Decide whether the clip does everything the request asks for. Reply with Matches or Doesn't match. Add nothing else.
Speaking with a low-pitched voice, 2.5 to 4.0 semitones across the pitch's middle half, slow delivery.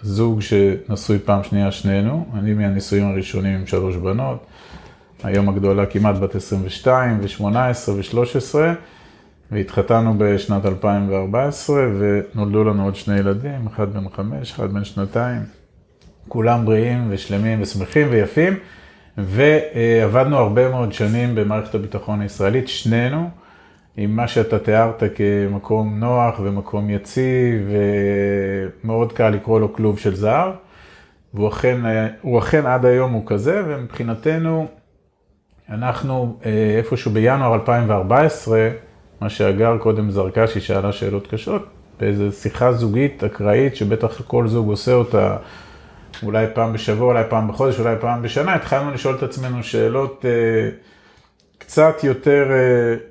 Doesn't match